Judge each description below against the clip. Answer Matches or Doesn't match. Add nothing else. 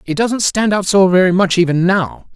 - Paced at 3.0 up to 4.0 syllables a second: Doesn't match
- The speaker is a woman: Doesn't match